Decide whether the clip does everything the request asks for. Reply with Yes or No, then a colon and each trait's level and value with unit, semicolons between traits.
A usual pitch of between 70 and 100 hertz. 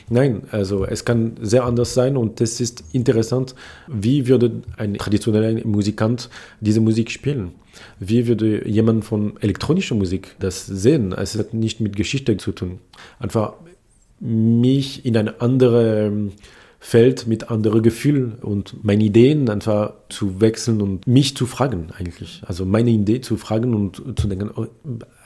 No: low, 110 Hz